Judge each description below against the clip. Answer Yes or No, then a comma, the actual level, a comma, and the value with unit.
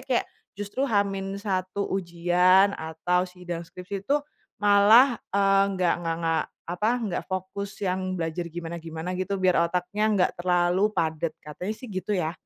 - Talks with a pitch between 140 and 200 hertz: Yes, medium, 185 Hz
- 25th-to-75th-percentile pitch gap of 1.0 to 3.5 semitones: Yes, narrow, 2.6 semitones